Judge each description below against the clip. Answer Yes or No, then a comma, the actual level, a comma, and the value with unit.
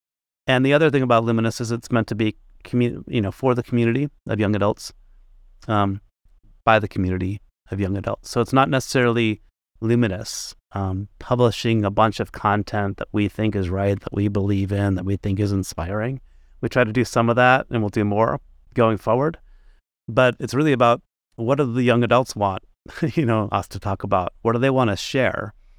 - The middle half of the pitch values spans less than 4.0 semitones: Yes, average, 3.5 semitones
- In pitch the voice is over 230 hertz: No, low, 110 Hz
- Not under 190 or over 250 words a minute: Yes, average, 200 wpm